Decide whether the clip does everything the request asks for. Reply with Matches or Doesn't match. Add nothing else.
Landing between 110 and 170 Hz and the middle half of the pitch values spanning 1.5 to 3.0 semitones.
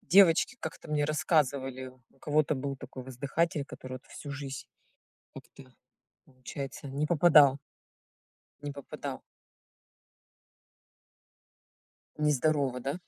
Matches